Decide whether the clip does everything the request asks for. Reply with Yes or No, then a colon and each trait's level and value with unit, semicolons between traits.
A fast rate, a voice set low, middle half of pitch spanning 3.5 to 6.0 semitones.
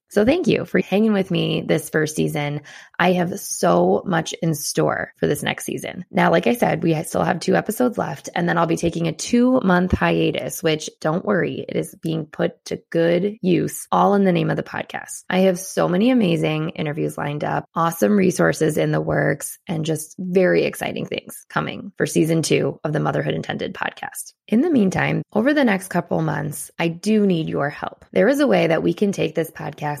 No: fast, 210 wpm; medium, 170 Hz; average, 3.8 semitones